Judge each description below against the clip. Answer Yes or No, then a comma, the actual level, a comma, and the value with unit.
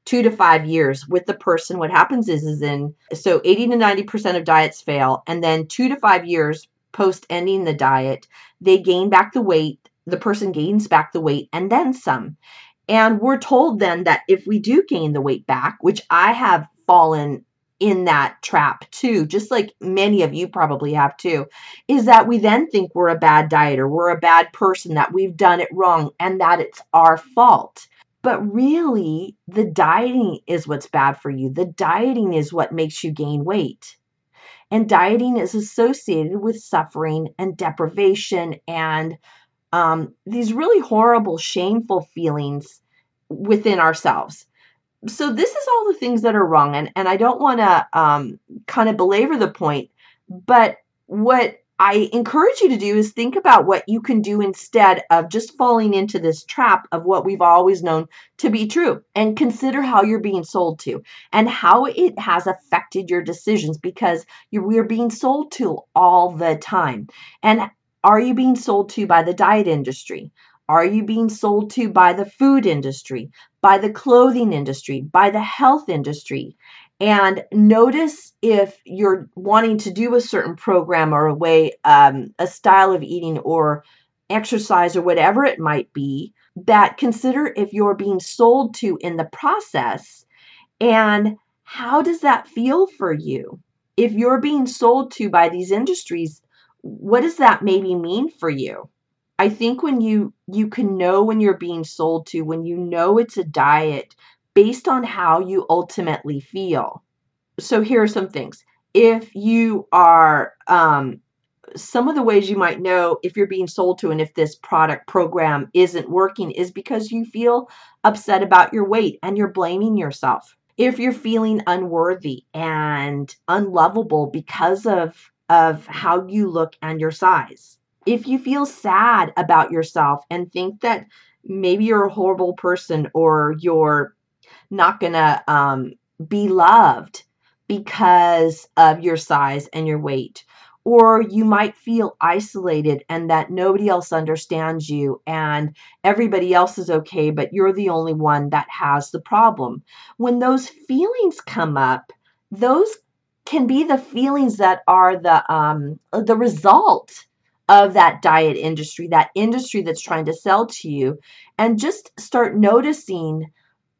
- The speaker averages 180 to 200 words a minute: No, average, 165 wpm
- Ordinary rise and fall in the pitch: No, wide, 5.8 semitones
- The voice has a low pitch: No, high, 190 Hz